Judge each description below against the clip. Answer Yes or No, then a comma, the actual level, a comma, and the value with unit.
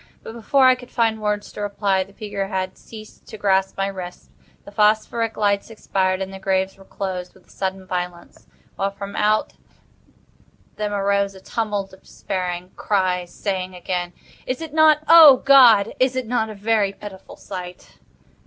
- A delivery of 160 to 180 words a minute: Yes, average, 170 wpm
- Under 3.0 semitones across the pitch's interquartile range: Yes, narrow, 2.6 semitones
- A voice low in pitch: No, high, 200 Hz